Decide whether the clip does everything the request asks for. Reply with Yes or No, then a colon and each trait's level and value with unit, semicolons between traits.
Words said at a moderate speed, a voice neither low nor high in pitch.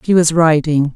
Yes: average, 190 wpm; medium, 160 Hz